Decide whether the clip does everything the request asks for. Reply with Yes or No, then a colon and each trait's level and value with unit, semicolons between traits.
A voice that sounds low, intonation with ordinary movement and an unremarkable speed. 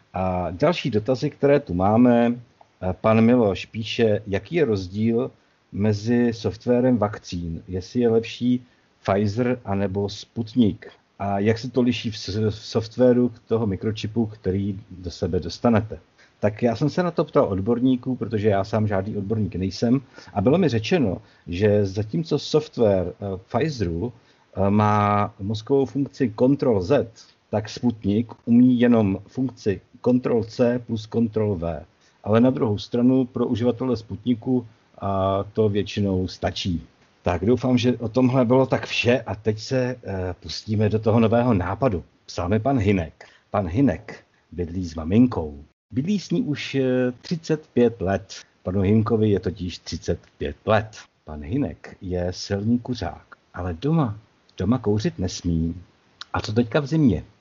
Yes: low, 110 Hz; average, 4.2 semitones; average, 140 wpm